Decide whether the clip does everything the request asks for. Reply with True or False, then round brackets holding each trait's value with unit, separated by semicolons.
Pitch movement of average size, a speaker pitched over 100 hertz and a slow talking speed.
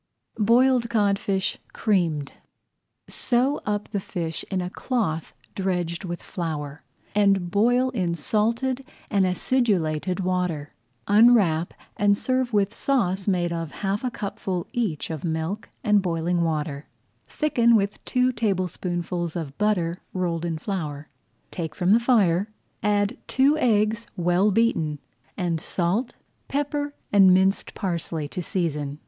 True (4.6 semitones; 190 Hz; 130 wpm)